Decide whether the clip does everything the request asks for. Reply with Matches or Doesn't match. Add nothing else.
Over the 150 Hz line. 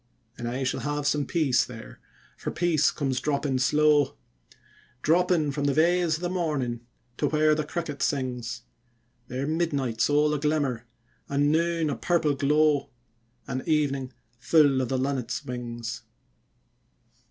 Doesn't match